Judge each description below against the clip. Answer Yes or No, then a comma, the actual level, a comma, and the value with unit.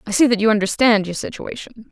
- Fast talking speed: Yes, fast, 220 wpm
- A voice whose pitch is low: No, high, 220 Hz